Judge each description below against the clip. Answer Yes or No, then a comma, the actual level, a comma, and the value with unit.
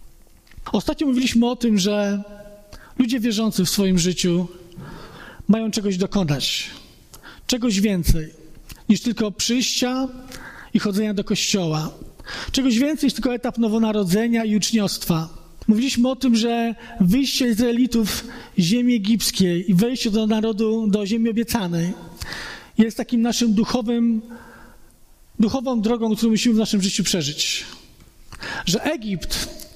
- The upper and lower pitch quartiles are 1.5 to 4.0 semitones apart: Yes, average, 2.9 semitones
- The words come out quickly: No, average, 120 wpm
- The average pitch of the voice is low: No, high, 220 Hz